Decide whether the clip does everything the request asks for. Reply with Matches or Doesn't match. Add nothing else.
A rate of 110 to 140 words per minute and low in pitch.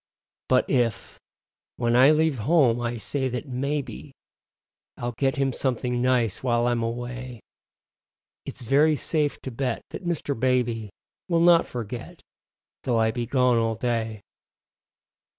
Matches